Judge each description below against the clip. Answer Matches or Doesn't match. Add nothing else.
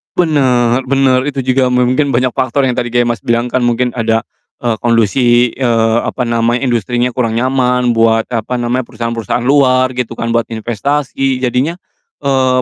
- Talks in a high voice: Doesn't match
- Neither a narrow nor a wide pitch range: Doesn't match